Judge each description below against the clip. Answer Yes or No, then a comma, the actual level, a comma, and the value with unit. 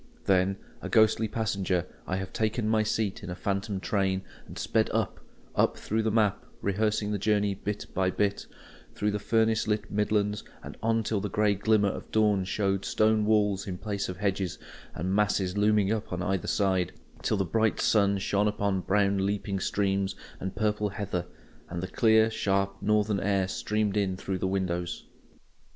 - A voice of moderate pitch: No, low, 100 Hz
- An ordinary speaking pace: Yes, average, 175 wpm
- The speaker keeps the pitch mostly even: Yes, narrow, 1.9 semitones